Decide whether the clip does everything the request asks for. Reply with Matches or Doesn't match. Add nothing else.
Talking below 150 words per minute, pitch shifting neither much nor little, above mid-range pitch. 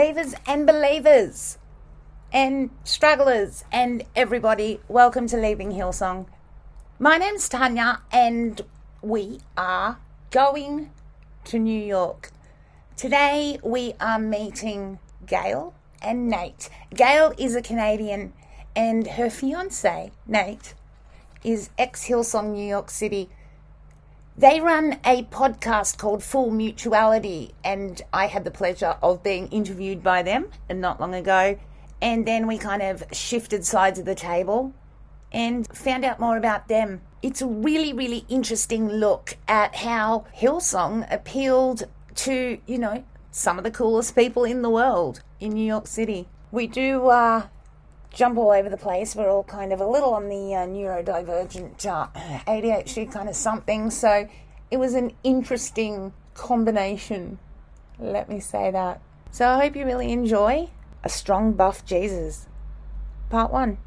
Matches